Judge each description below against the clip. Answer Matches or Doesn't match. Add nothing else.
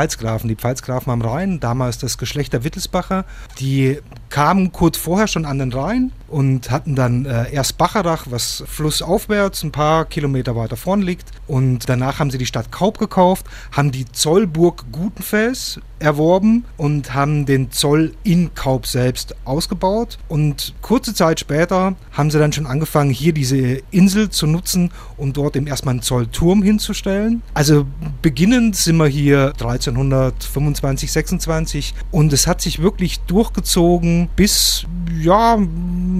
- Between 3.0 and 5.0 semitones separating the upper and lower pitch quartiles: Doesn't match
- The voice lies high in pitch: Doesn't match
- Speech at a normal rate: Matches